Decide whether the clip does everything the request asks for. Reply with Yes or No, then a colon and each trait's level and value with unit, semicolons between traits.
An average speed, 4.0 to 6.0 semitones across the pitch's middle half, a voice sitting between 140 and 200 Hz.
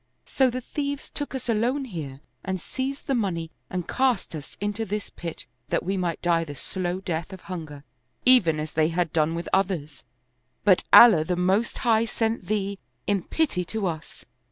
Yes: average, 180 wpm; wide, 5.4 semitones; high, 190 Hz